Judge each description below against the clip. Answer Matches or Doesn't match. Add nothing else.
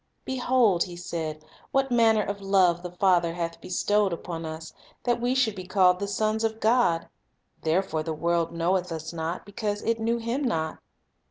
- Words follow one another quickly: Doesn't match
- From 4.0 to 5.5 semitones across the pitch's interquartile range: Matches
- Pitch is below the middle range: Doesn't match